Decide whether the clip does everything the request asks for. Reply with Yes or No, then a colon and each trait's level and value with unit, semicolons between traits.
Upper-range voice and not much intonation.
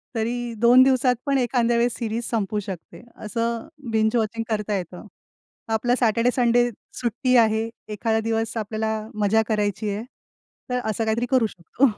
Yes: high, 225 Hz; narrow, 1.9 semitones